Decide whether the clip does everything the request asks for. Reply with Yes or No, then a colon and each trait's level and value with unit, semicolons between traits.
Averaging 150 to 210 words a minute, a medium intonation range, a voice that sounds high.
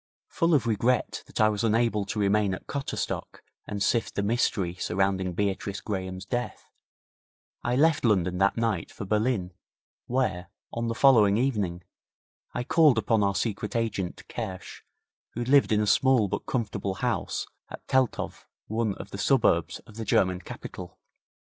No: average, 155 wpm; average, 3.7 semitones; low, 105 Hz